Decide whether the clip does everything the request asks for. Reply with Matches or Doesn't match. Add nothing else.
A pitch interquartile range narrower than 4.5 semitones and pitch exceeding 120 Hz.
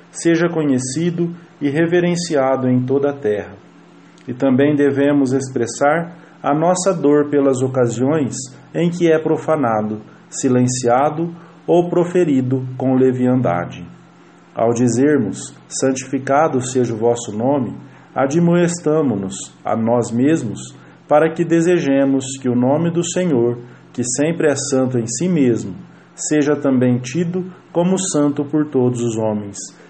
Doesn't match